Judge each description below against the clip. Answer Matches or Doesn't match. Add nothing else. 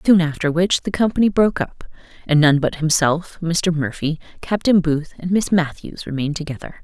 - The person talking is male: Doesn't match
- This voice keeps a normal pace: Matches